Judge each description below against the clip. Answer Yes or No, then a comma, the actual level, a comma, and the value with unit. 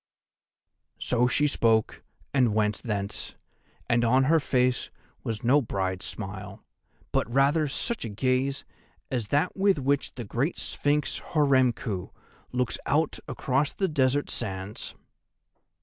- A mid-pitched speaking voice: No, low, 125 Hz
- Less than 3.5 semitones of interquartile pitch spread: No, average, 4.5 semitones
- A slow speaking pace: Yes, slow, 125 wpm